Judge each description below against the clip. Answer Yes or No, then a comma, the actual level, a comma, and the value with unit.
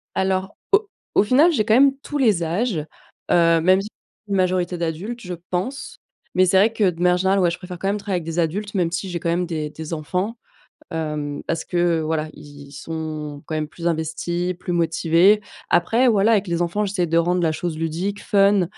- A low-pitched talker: No, medium, 180 Hz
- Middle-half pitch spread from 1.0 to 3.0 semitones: No, average, 3.6 semitones